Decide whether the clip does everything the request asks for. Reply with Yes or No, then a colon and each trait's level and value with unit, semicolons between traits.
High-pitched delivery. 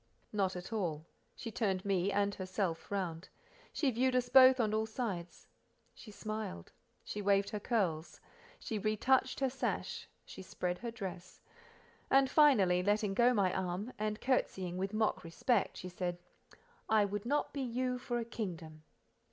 Yes: high, 205 Hz